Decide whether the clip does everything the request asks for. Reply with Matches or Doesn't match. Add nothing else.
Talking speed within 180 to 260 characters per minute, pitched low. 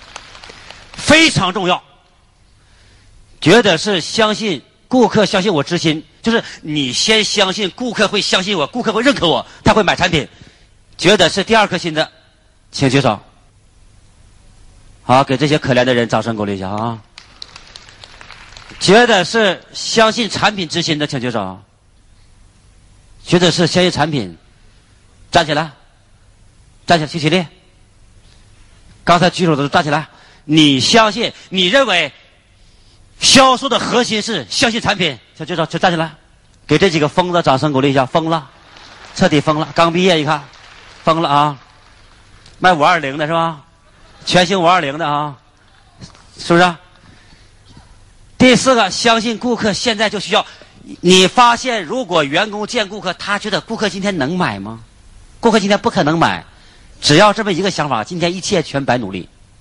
Doesn't match